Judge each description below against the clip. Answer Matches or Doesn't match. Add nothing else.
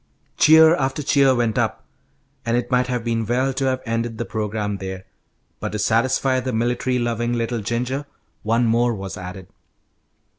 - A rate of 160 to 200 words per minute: Matches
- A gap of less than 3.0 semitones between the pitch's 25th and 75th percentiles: Matches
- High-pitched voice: Doesn't match